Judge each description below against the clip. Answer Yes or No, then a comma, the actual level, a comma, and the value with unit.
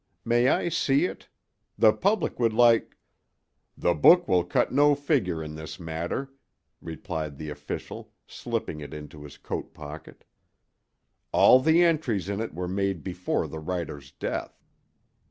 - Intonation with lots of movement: Yes, wide, 8.9 semitones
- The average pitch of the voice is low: Yes, very low, 90 Hz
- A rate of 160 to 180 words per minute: No, average, 145 wpm